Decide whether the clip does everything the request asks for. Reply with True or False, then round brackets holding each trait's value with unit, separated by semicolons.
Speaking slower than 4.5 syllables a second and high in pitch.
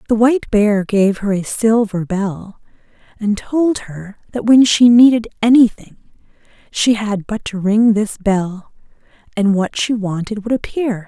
True (4.2 syllables/s; 215 Hz)